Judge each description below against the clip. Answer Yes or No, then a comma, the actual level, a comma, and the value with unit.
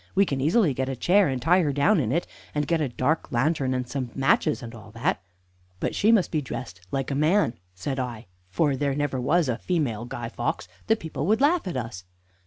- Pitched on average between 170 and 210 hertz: No, medium, 140 Hz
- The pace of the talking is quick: Yes, fast, 220 wpm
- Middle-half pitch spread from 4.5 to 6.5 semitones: Yes, average, 5.1 semitones